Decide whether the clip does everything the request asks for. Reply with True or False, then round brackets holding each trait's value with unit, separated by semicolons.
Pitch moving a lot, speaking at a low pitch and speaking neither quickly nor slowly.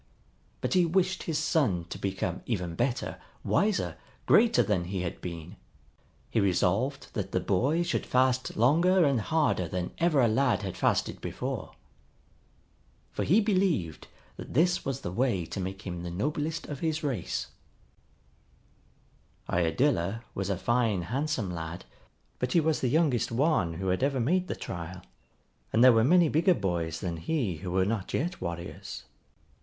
True (9.0 semitones; 120 Hz; 160 wpm)